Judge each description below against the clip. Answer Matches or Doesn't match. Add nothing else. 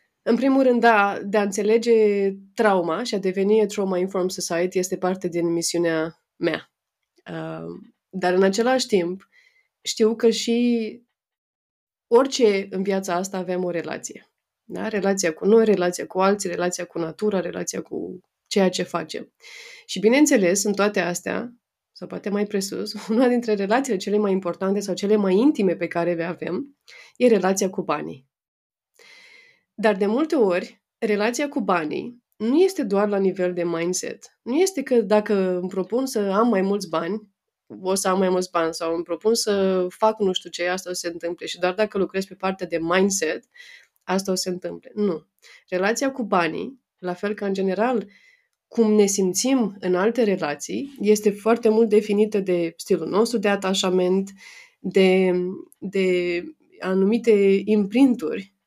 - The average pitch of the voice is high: Matches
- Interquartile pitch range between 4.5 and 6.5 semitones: Doesn't match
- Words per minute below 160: Doesn't match